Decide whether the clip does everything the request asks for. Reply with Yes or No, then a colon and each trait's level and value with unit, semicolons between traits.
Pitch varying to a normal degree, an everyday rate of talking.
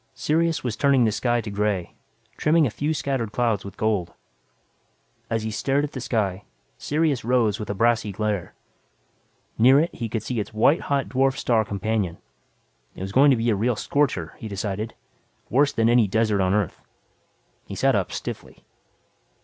Yes: average, 4.3 semitones; average, 175 wpm